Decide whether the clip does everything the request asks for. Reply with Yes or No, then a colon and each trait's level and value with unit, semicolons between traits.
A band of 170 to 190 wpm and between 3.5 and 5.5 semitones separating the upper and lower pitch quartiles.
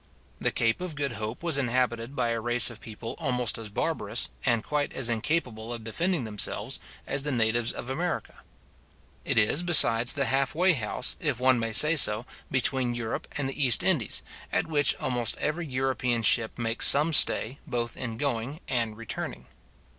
Yes: average, 175 wpm; average, 3.8 semitones